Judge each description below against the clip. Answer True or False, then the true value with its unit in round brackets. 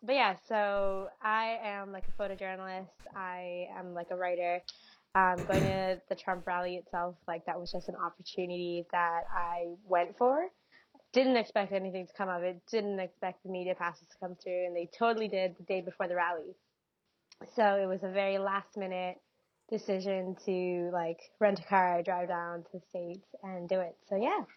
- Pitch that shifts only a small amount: True (1.7 semitones)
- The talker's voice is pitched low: False (185 Hz)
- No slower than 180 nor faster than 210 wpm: True (190 wpm)